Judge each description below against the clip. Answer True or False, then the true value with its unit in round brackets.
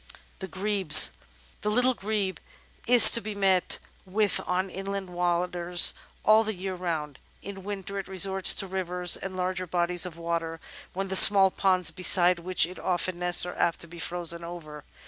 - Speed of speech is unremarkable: True (170 wpm)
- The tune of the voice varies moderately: False (1.9 semitones)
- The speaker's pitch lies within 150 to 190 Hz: True (185 Hz)